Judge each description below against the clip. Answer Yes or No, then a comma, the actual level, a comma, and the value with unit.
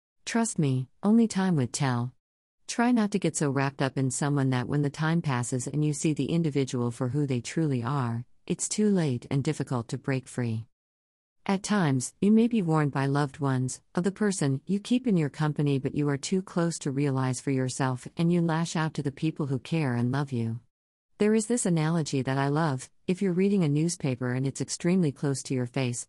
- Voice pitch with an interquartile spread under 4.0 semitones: No, average, 4.5 semitones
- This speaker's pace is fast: Yes, fast, 220 wpm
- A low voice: No, medium, 145 Hz